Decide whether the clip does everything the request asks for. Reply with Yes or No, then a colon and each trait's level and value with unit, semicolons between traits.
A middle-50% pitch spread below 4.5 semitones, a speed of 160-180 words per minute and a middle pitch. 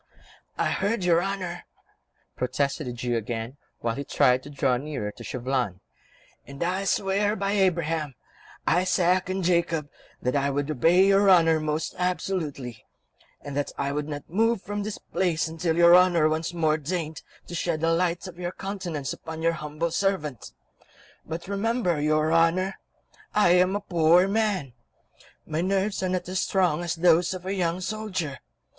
Yes: average, 3.8 semitones; average, 165 wpm; medium, 170 Hz